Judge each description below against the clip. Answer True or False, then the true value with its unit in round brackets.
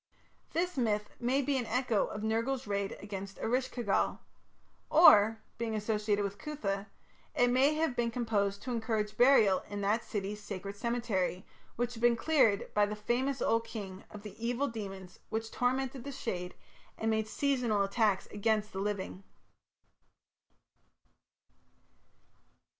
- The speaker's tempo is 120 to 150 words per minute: True (145 wpm)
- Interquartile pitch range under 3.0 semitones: False (3.3 semitones)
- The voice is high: True (220 Hz)